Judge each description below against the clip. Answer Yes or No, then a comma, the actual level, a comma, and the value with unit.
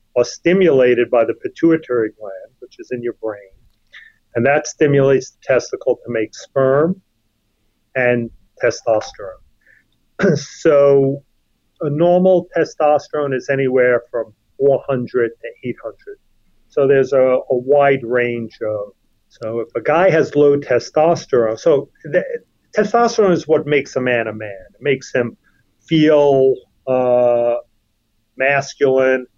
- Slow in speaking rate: Yes, slow, 125 wpm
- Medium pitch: No, low, 130 Hz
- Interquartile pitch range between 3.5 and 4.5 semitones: Yes, average, 4.1 semitones